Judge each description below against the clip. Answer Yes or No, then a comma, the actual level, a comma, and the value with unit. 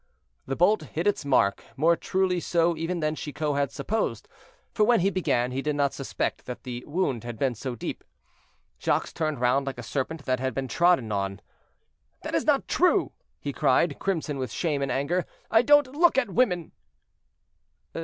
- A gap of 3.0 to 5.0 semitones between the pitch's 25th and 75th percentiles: No, wide, 5.4 semitones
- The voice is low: No, medium, 150 Hz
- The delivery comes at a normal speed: Yes, average, 185 wpm